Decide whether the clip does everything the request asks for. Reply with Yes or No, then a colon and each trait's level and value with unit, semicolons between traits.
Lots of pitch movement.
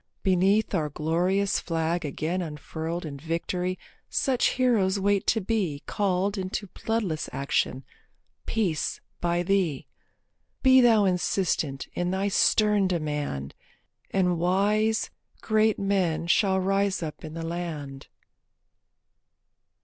No: average, 3.7 semitones